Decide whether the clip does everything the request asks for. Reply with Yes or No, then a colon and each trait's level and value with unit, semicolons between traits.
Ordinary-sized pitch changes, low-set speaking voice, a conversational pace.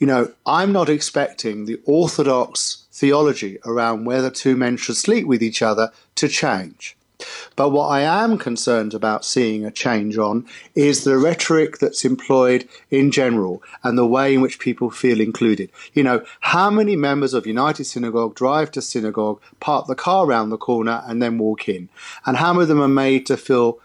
Yes: average, 3.7 semitones; low, 125 Hz; average, 185 wpm